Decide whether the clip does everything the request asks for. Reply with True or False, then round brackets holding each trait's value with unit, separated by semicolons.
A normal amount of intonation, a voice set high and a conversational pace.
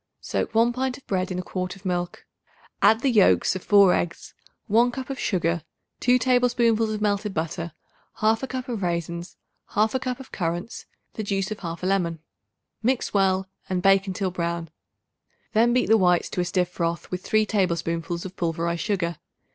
True (4.4 semitones; 195 Hz; 180 wpm)